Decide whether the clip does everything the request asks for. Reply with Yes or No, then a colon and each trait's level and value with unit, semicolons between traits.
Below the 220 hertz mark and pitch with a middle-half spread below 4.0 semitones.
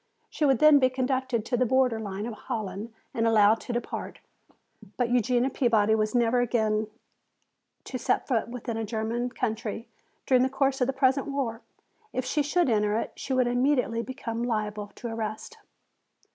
No: high, 240 Hz; average, 2.8 semitones